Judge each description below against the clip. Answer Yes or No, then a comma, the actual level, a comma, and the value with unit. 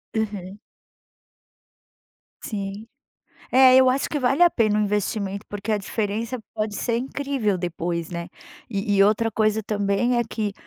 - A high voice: Yes, high, 215 Hz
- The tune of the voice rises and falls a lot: No, average, 3.0 semitones